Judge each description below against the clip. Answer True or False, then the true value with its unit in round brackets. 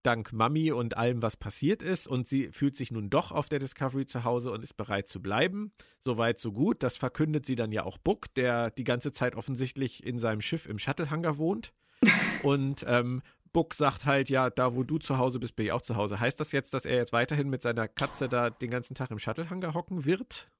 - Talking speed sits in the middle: False (230 wpm)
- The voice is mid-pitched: False (130 Hz)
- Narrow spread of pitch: False (3.9 semitones)